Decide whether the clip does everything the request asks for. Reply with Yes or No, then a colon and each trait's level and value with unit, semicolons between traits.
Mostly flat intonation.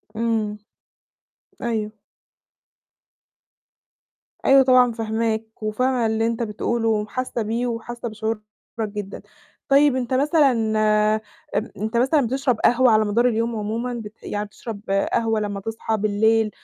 Yes: narrow, 2.2 semitones